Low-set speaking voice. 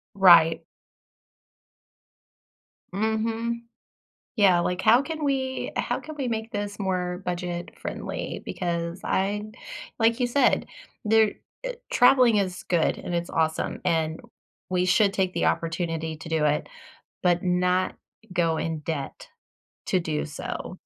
No: medium, 185 Hz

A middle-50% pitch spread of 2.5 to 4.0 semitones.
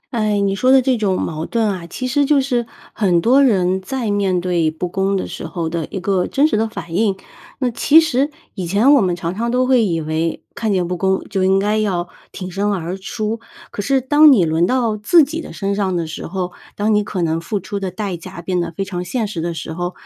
No: average, 4.6 semitones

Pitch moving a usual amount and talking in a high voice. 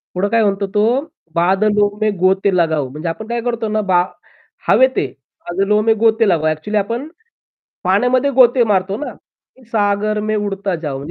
Yes: average, 3.2 semitones; high, 205 Hz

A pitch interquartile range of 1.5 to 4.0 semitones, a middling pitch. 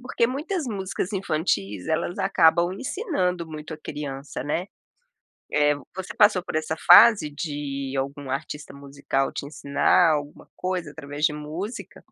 No: average, 4.4 semitones; medium, 155 Hz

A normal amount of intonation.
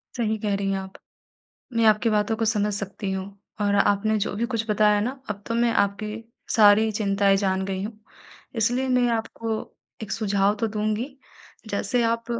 No: narrow, 2.1 semitones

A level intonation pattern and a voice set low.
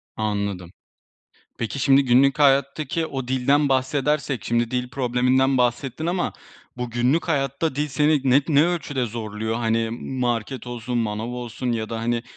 No: average, 3.1 semitones; low, 125 Hz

